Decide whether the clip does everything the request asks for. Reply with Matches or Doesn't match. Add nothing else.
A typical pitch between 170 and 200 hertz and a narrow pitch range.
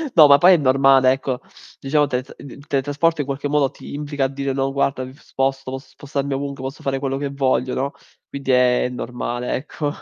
Doesn't match